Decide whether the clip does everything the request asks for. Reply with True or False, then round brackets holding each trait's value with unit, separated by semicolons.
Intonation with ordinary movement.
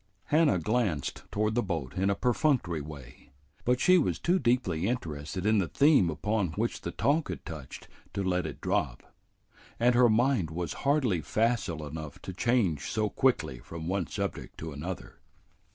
False (7.2 semitones)